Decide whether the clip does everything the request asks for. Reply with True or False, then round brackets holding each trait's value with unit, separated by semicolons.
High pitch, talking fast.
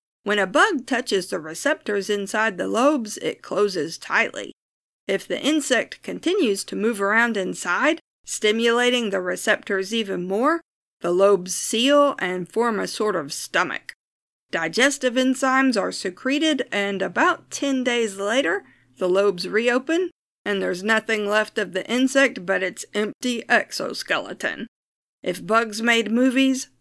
False (230 Hz; 135 wpm)